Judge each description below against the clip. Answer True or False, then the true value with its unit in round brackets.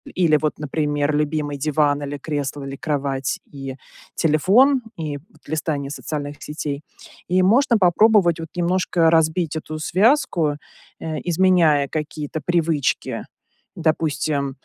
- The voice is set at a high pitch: False (155 Hz)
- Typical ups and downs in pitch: True (3.0 semitones)